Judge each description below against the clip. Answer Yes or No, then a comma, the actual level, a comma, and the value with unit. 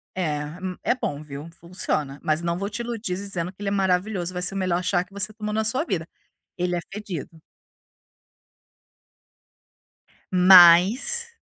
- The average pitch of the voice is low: No, medium, 185 Hz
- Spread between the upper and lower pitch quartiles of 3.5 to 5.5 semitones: No, average, 3.1 semitones